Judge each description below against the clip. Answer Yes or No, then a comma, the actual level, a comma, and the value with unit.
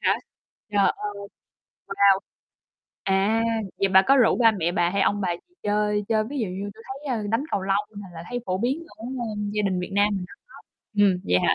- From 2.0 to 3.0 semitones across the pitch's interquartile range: Yes, narrow, 2.6 semitones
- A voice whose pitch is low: No, high, 205 Hz